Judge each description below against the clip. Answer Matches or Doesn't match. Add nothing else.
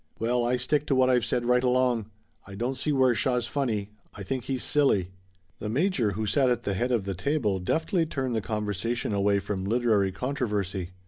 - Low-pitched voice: Matches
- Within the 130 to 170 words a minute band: Doesn't match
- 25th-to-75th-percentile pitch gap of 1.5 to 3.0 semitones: Doesn't match